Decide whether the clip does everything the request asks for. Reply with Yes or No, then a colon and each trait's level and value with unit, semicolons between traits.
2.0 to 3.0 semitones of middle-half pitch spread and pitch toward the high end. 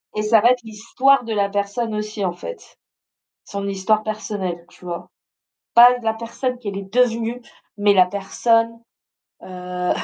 Yes: average, 2.7 semitones; high, 215 Hz